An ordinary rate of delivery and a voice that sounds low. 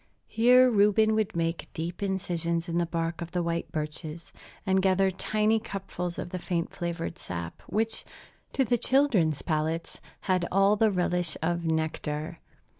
No: average, 155 wpm; medium, 175 Hz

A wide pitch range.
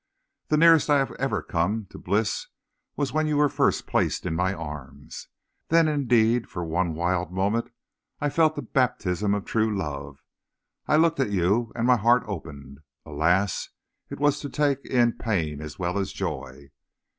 Yes: wide, 8.3 semitones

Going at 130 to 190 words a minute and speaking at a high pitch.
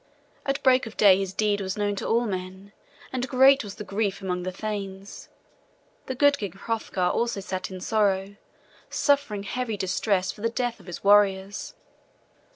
Yes: average, 170 wpm; high, 205 Hz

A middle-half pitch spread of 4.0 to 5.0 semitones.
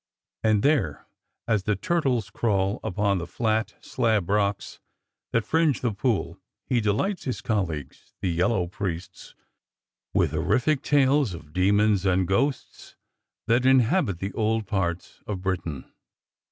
Yes: average, 4.4 semitones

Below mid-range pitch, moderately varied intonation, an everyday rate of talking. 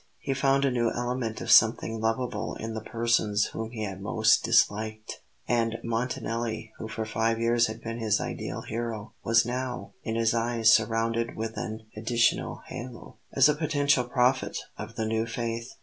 No: low, 115 Hz; narrow, 1.5 semitones; average, 170 wpm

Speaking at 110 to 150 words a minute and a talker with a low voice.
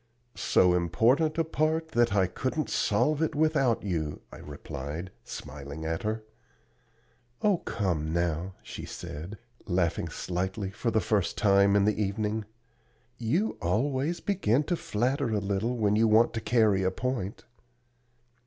Yes: average, 145 wpm; low, 105 Hz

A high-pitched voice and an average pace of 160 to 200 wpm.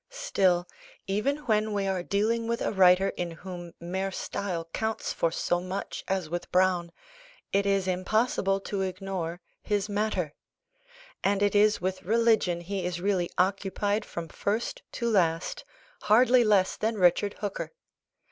No: high, 195 Hz; average, 145 wpm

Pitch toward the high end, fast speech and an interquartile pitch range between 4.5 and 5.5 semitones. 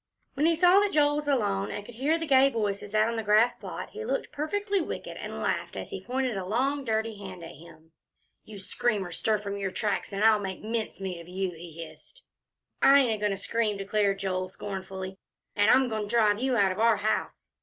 Yes: high, 215 Hz; fast, 235 wpm; average, 5.2 semitones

